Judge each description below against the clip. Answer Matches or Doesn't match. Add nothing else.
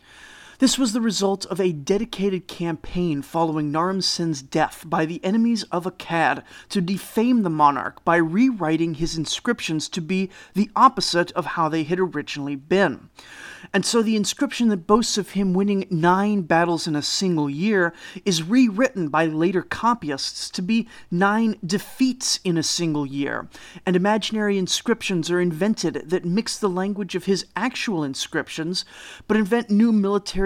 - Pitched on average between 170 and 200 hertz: Matches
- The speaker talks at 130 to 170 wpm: Matches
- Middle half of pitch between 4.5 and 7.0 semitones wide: Doesn't match